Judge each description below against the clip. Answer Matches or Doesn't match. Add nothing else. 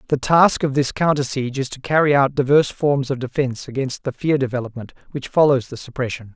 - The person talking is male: Matches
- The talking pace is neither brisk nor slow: Doesn't match